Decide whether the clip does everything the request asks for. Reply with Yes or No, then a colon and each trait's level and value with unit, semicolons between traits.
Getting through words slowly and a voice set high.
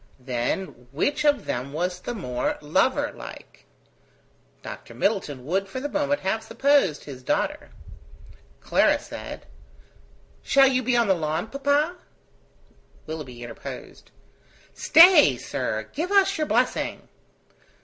Yes: slow, 120 wpm; high, 195 Hz